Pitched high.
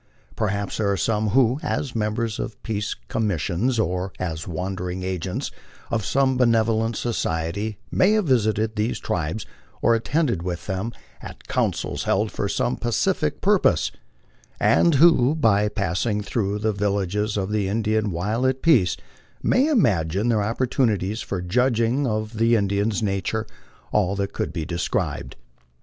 No: low, 105 Hz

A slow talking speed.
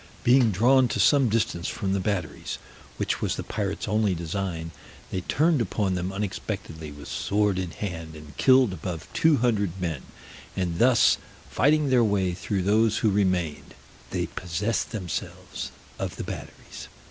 No: average, 155 wpm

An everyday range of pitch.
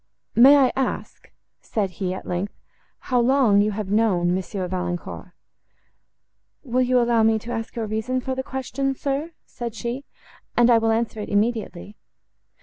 Yes: average, 3.8 semitones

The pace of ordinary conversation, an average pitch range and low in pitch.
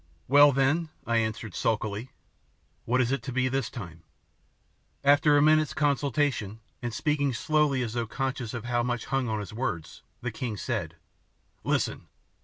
Yes: average, 160 wpm; average, 3.8 semitones; low, 125 Hz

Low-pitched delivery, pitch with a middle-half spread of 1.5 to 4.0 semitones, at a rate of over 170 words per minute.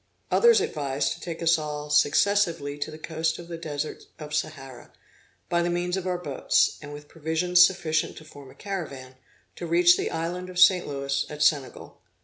No: medium, 160 Hz; average, 3.2 semitones; average, 185 wpm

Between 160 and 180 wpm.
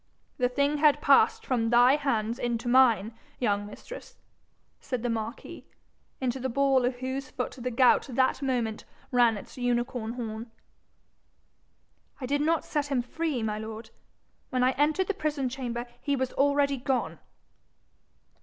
No: average, 150 wpm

